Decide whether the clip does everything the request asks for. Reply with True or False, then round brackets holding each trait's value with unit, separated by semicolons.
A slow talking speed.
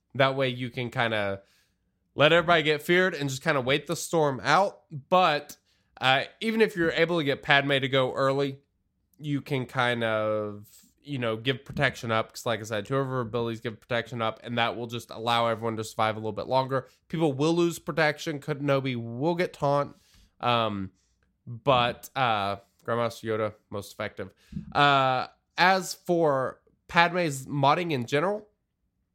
False (175 wpm)